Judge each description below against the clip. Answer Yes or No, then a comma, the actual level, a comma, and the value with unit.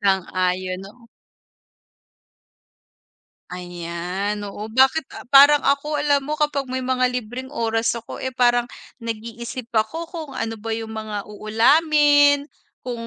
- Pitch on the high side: Yes, high, 235 Hz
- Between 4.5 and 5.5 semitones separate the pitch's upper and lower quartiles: Yes, average, 4.9 semitones